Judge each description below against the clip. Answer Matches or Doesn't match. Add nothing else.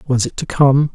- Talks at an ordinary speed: Doesn't match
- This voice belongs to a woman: Doesn't match